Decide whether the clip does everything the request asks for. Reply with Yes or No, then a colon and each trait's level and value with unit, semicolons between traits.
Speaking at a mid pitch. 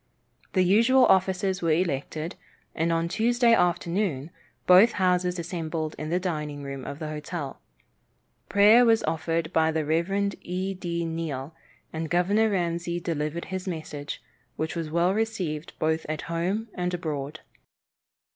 Yes: medium, 170 Hz